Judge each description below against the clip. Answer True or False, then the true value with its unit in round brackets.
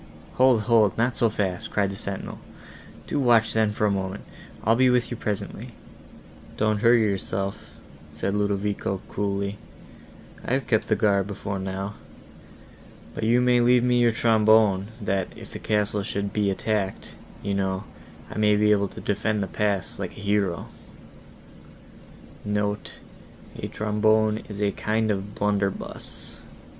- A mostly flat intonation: True (1.8 semitones)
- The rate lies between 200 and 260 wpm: False (140 wpm)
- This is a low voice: True (105 Hz)